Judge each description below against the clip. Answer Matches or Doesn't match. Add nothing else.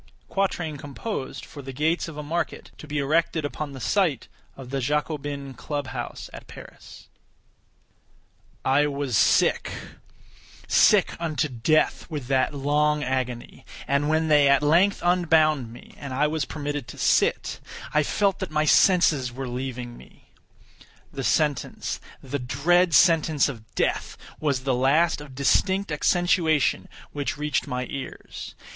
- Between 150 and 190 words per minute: Doesn't match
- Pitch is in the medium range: Matches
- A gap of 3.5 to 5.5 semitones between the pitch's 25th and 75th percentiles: Doesn't match